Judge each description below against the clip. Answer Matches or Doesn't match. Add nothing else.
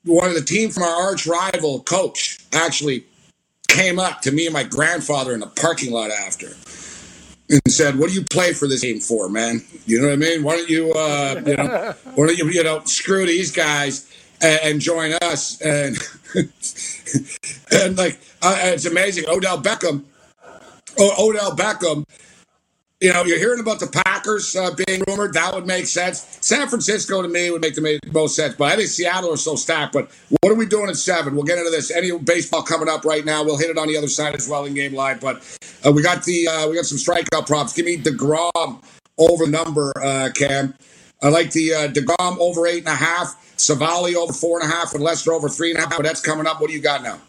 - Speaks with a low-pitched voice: Doesn't match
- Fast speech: Matches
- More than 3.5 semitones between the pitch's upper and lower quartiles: Doesn't match